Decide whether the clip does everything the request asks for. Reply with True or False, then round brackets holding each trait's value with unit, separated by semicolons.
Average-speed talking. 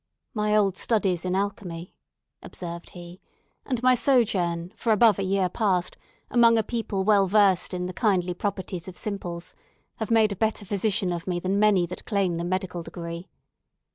True (170 wpm)